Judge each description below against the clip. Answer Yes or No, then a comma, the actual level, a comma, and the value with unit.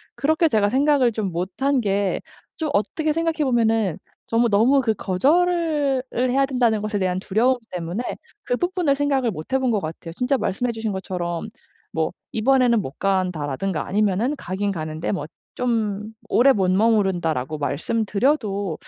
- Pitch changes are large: Yes, wide, 5.8 semitones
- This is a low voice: No, high, 220 Hz